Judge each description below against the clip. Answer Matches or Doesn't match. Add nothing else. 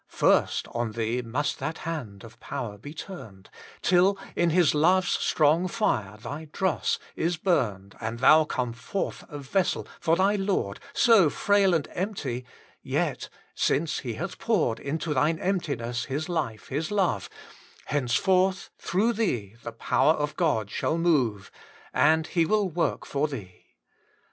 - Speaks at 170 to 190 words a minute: Doesn't match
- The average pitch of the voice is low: Doesn't match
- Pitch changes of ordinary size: Doesn't match